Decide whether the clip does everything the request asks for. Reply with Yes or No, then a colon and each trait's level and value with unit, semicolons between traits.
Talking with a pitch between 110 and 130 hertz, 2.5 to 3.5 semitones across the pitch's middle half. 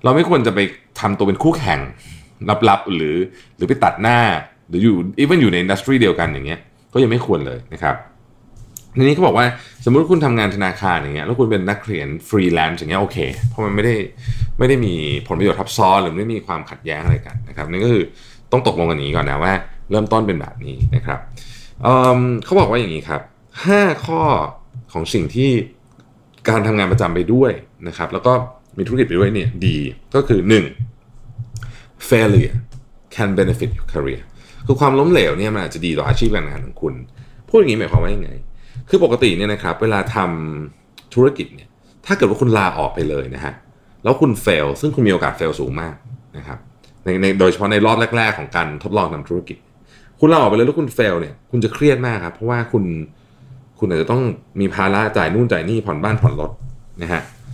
No: low, 115 Hz; average, 4.4 semitones